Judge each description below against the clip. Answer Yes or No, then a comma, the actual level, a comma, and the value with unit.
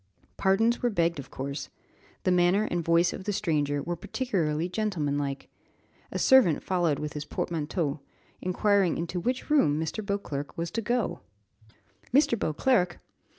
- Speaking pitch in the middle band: Yes, medium, 175 Hz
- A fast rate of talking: No, average, 145 wpm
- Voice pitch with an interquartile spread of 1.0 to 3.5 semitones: No, average, 5.3 semitones